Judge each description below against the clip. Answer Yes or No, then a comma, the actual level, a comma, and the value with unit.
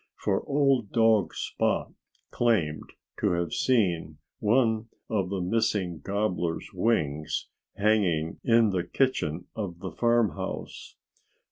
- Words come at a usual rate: No, slow, 110 wpm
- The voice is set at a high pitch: No, low, 100 Hz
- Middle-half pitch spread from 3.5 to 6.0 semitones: Yes, average, 4.7 semitones